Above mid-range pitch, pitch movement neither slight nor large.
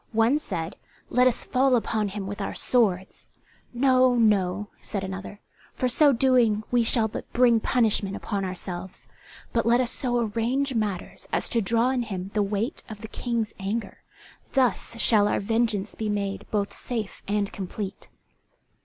Yes: high, 220 Hz; average, 3.3 semitones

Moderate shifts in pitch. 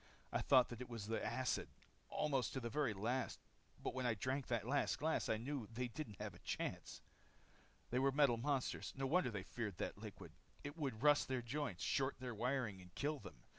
Yes: average, 3.7 semitones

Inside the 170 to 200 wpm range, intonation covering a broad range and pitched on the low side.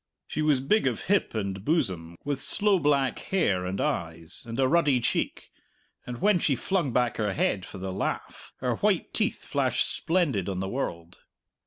Yes: average, 180 wpm; wide, 8.1 semitones; low, 125 Hz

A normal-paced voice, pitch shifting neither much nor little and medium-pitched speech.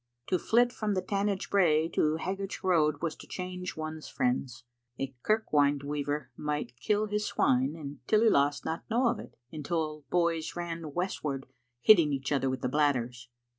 Yes: average, 165 wpm; average, 4.7 semitones; medium, 155 Hz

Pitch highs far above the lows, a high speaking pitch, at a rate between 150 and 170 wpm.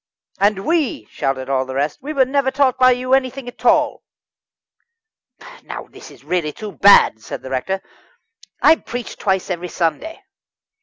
Yes: wide, 8.6 semitones; high, 210 Hz; average, 155 wpm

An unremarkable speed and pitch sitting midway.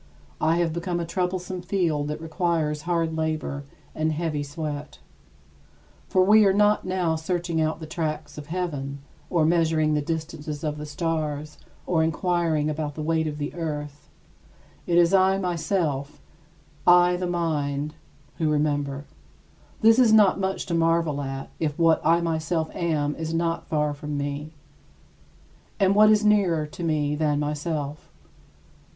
Yes: average, 150 wpm; medium, 160 Hz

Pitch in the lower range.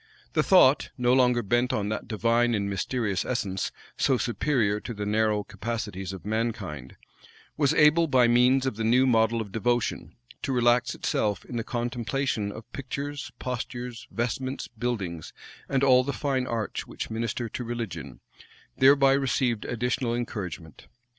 Yes: low, 120 Hz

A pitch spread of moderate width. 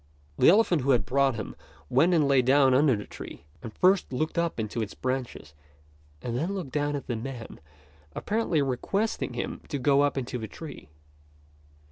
Yes: average, 4.2 semitones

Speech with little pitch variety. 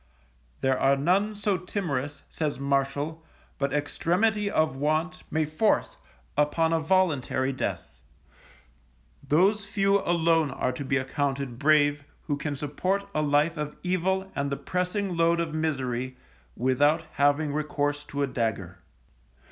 No: average, 4.1 semitones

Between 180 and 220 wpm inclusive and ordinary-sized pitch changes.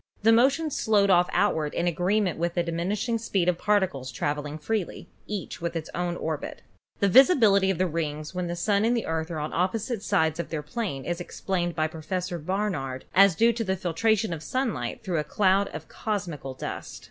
Yes: average, 200 wpm; average, 4.5 semitones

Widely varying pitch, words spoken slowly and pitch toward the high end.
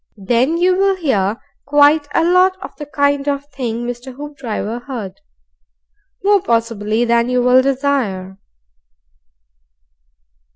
No: average, 4.0 semitones; slow, 120 wpm; very high, 260 Hz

